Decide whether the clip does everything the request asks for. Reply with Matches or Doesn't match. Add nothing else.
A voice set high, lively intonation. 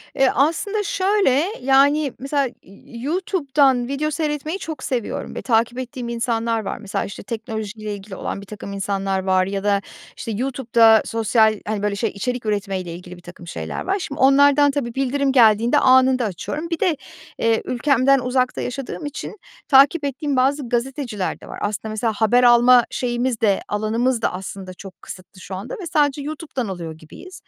Doesn't match